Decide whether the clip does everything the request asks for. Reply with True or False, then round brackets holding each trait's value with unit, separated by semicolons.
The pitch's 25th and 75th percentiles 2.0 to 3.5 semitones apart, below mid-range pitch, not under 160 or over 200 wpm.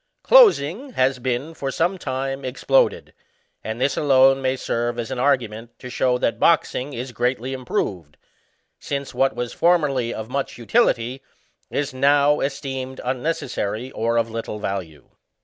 False (2.9 semitones; 130 Hz; 145 wpm)